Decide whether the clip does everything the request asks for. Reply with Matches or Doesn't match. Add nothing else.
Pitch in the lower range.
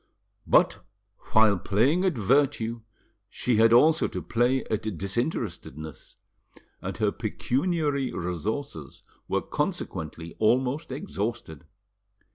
Matches